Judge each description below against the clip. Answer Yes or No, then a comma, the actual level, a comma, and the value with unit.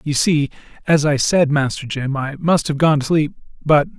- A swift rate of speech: Yes, fast, 210 wpm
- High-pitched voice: No, medium, 150 Hz